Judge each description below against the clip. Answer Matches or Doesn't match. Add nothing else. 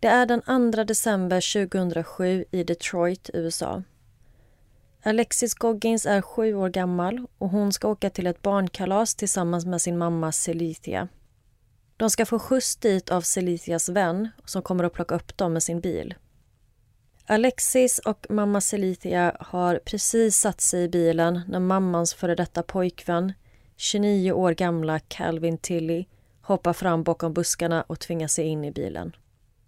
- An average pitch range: Matches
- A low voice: Doesn't match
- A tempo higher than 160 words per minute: Doesn't match